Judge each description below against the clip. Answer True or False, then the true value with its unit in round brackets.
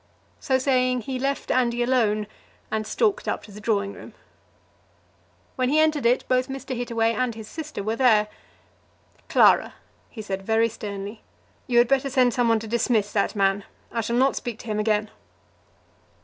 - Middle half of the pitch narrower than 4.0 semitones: True (3.2 semitones)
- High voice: True (235 Hz)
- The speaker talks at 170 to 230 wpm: True (175 wpm)